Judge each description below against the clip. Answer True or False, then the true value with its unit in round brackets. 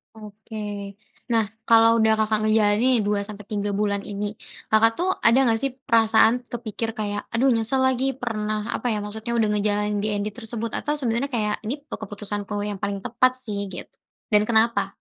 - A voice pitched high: True (220 Hz)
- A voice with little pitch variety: True (2.0 semitones)